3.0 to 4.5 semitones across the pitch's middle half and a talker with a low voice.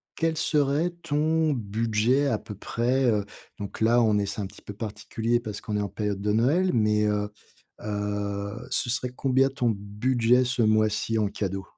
Yes: average, 3.7 semitones; low, 110 Hz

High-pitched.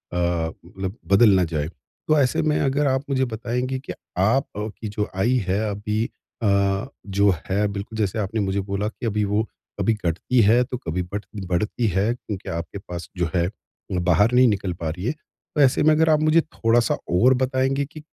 No: low, 105 Hz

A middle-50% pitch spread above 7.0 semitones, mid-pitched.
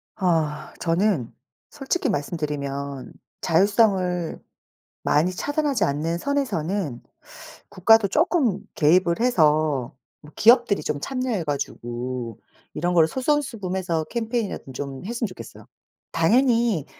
Yes: wide, 7.4 semitones; medium, 180 Hz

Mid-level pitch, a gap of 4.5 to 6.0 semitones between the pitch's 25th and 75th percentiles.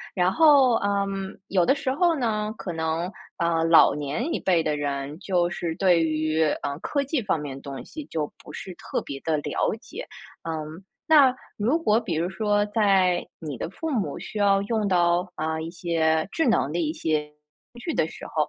Yes: medium, 180 Hz; average, 5.0 semitones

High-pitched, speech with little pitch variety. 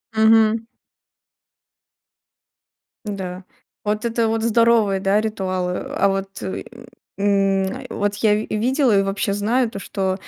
Yes: high, 205 Hz; narrow, 2.3 semitones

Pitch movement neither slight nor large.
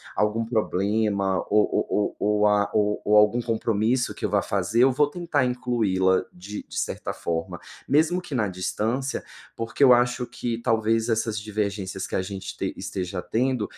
Yes: average, 3.1 semitones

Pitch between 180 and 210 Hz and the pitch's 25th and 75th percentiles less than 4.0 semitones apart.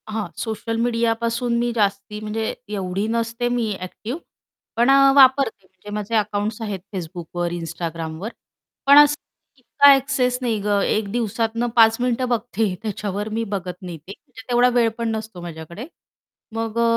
No: high, 225 Hz; average, 3.2 semitones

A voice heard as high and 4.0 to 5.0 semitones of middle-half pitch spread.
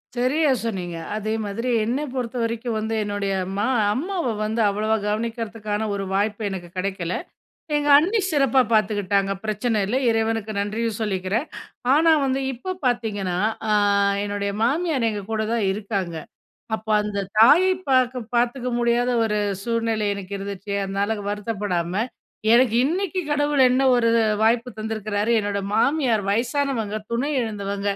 No: high, 220 Hz; average, 3.3 semitones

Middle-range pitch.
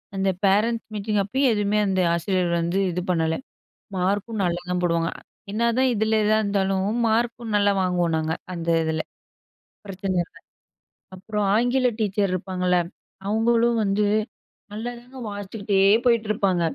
No: high, 200 Hz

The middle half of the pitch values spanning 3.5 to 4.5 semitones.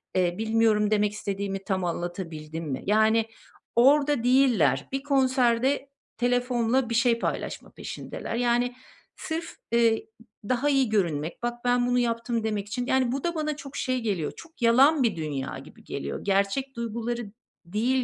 Yes: average, 4.2 semitones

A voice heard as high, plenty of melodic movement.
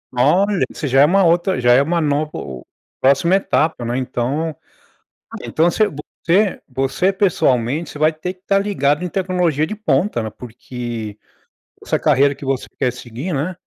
No: medium, 150 Hz; wide, 5.9 semitones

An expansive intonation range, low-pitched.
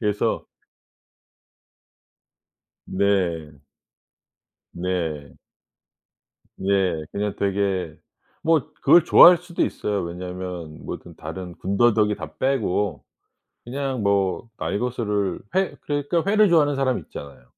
Yes: wide, 6.5 semitones; low, 100 Hz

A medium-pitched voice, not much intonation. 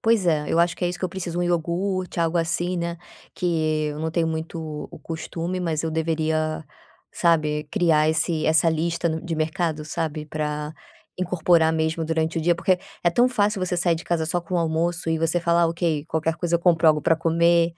Yes: medium, 165 Hz; narrow, 1.6 semitones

